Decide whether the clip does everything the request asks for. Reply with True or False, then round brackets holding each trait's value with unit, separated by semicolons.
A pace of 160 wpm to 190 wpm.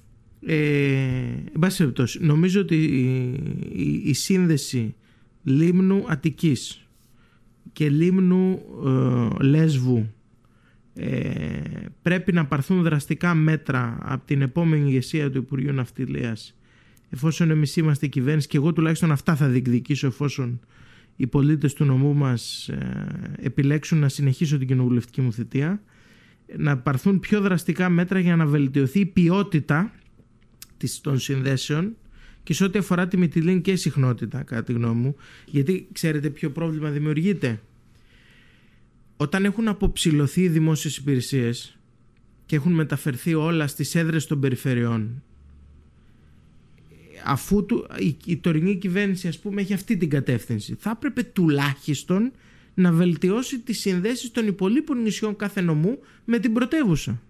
False (125 wpm)